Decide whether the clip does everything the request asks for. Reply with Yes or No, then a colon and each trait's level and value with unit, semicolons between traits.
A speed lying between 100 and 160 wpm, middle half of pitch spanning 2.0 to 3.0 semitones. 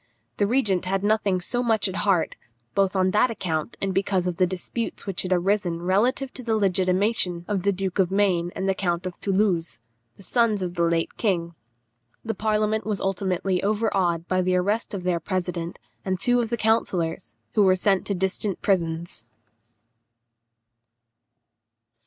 No: average, 170 wpm; average, 2.7 semitones